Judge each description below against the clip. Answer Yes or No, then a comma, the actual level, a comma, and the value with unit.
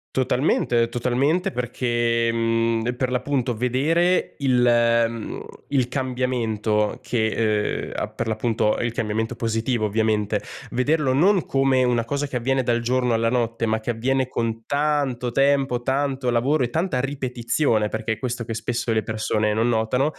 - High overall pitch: No, low, 120 Hz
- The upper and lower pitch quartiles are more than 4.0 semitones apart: No, narrow, 2.6 semitones